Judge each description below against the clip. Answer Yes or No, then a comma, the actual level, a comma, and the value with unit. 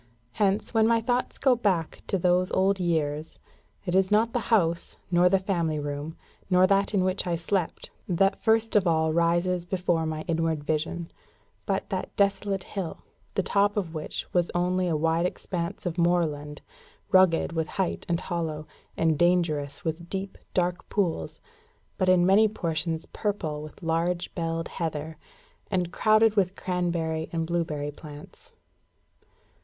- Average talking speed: Yes, average, 155 wpm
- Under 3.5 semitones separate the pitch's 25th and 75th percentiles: Yes, average, 2.9 semitones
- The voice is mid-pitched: Yes, medium, 175 Hz